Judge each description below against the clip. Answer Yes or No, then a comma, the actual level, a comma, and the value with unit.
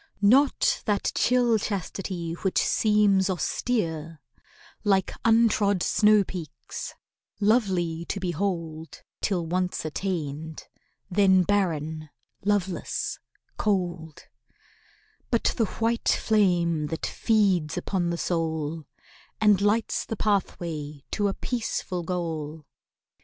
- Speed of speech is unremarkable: No, slow, 95 wpm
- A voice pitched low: No, medium, 185 Hz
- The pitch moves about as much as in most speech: Yes, average, 4.2 semitones